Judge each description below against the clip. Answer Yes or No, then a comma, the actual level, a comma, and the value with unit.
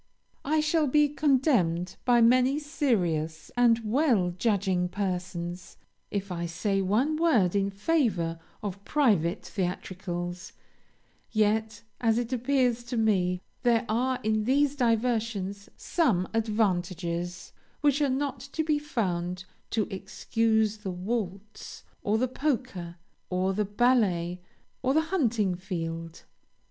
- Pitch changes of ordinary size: No, wide, 5.7 semitones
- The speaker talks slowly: Yes, slow, 120 wpm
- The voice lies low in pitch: No, high, 215 Hz